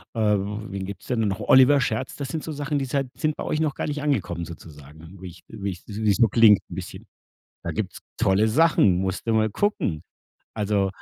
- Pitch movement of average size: No, wide, 5.9 semitones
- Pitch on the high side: No, low, 110 Hz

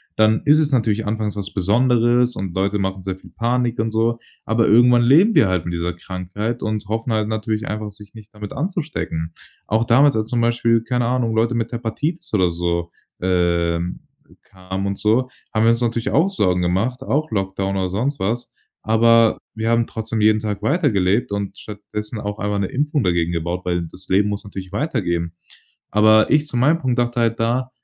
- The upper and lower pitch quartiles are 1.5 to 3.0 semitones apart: No, average, 3.8 semitones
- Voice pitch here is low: Yes, low, 110 Hz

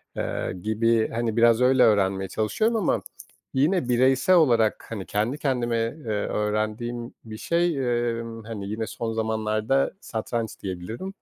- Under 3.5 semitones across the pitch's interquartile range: Yes, average, 2.8 semitones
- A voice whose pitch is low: Yes, low, 115 Hz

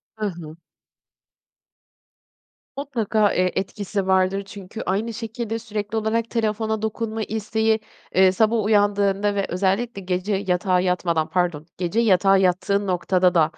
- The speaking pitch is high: Yes, high, 200 Hz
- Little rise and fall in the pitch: No, average, 3.0 semitones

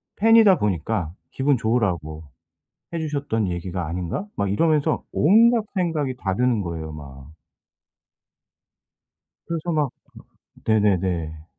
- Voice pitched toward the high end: No, low, 110 Hz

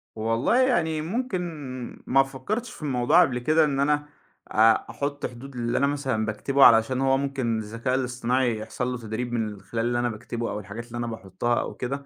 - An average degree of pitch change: Yes, average, 3.4 semitones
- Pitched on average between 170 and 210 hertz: No, low, 125 Hz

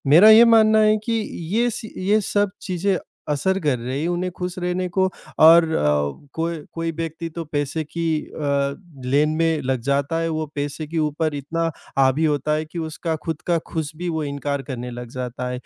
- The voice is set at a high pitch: No, medium, 160 Hz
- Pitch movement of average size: Yes, average, 3.1 semitones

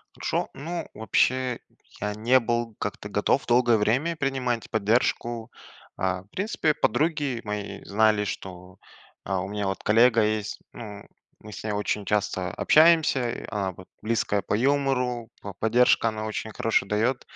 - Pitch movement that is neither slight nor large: Yes, average, 3.4 semitones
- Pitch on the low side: Yes, low, 115 Hz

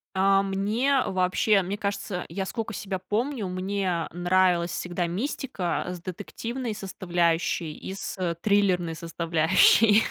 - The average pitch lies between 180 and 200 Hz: Yes, high, 190 Hz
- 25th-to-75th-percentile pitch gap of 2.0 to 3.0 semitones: Yes, average, 2.7 semitones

